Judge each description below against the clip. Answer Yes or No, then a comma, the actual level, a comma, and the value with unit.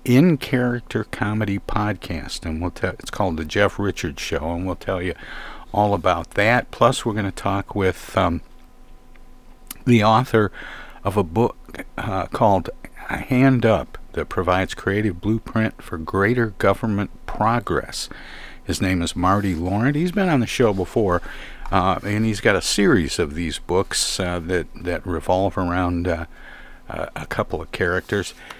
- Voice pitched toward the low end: Yes, low, 100 Hz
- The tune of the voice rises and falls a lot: No, average, 3.8 semitones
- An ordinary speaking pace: Yes, average, 150 wpm